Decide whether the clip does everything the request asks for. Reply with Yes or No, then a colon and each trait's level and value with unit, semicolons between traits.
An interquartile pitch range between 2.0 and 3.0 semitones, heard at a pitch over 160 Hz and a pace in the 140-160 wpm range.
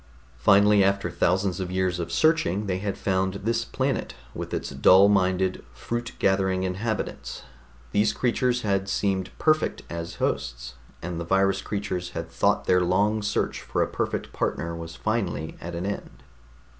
No: average, 2.7 semitones; very low, 95 Hz; average, 155 wpm